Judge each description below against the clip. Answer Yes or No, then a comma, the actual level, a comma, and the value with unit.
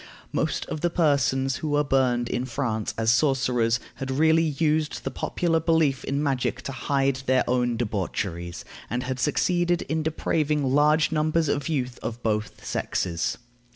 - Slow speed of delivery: No, average, 155 wpm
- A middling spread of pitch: Yes, average, 3.9 semitones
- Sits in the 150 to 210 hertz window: No, low, 135 Hz